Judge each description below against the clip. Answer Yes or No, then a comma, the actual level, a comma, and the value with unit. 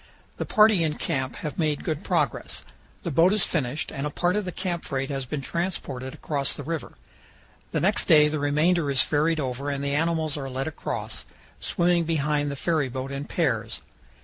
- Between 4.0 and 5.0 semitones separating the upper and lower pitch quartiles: No, average, 3.2 semitones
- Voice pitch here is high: No, medium, 150 Hz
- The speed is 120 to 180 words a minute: No, average, 190 wpm